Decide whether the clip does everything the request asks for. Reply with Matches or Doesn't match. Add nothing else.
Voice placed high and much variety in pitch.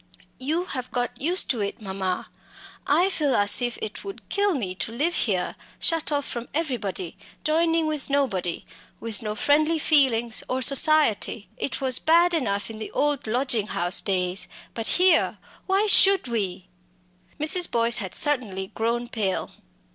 Matches